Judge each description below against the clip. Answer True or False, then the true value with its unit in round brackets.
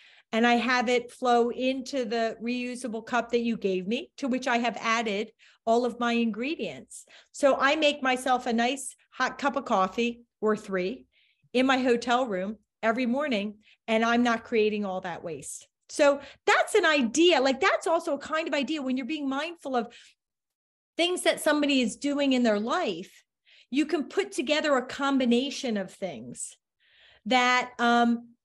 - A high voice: True (245 Hz)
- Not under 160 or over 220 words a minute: True (170 wpm)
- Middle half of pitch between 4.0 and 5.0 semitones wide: False (3.2 semitones)